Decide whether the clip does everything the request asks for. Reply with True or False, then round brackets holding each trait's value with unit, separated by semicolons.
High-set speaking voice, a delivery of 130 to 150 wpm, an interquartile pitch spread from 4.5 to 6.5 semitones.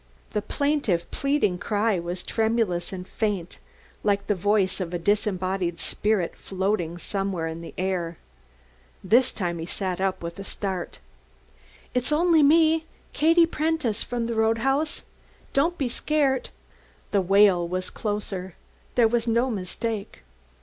True (205 Hz; 135 wpm; 4.9 semitones)